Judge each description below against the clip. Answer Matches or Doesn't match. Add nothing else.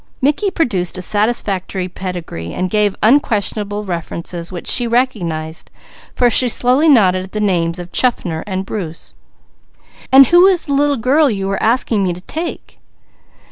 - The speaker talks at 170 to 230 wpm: Doesn't match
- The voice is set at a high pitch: Matches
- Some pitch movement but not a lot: Doesn't match